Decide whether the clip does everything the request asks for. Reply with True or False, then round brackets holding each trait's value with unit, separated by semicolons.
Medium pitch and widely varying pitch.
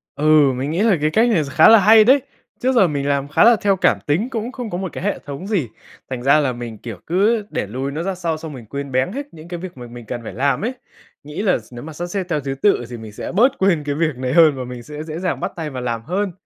True (155 Hz; 6.6 semitones)